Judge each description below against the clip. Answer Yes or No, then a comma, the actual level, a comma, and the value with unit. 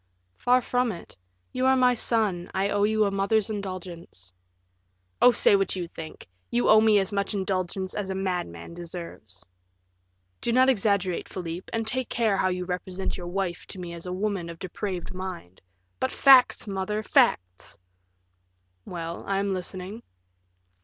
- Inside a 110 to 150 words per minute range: No, average, 165 wpm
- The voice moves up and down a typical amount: Yes, average, 3.5 semitones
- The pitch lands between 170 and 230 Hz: Yes, high, 190 Hz